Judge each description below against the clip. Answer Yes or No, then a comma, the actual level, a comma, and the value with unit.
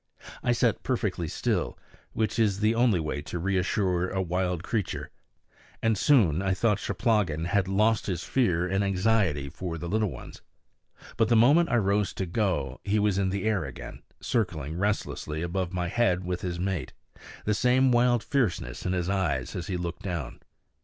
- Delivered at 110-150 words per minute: No, average, 180 wpm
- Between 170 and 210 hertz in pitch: No, very low, 95 Hz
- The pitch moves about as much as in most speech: Yes, average, 3.8 semitones